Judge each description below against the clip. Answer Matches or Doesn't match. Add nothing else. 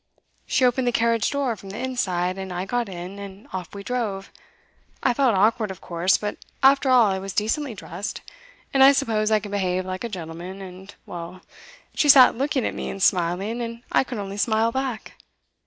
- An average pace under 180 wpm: Doesn't match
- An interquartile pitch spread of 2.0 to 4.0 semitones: Doesn't match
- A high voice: Matches